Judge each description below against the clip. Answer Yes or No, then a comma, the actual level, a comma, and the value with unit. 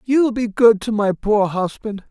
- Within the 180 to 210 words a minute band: No, fast, 230 wpm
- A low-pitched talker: No, high, 220 Hz